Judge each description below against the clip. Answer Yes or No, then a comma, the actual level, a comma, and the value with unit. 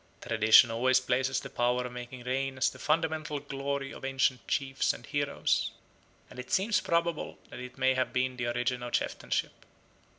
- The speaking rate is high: No, average, 175 wpm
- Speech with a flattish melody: Yes, narrow, 2.0 semitones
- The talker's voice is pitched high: No, low, 130 Hz